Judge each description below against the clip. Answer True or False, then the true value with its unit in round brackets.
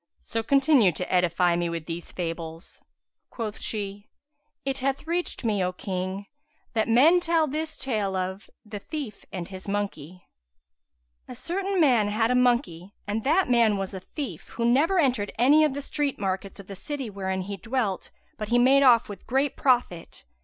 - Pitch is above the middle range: True (220 Hz)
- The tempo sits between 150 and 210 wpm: True (175 wpm)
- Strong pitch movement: True (6.3 semitones)